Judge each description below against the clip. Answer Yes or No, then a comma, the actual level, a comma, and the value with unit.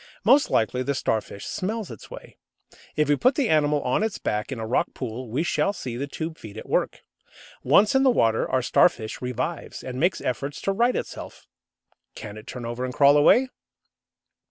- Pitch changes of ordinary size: No, wide, 7.3 semitones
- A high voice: No, medium, 140 Hz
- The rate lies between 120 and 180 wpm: No, average, 195 wpm